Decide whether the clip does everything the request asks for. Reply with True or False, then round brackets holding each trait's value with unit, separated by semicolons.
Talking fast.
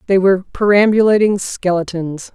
False (105 wpm)